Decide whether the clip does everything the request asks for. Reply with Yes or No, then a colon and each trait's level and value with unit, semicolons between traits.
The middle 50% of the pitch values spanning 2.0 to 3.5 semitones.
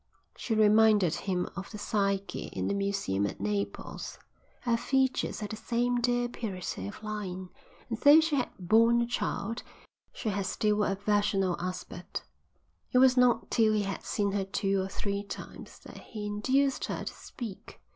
Yes: average, 3.2 semitones